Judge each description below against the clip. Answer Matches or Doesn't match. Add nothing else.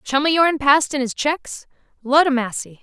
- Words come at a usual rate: Matches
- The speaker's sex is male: Doesn't match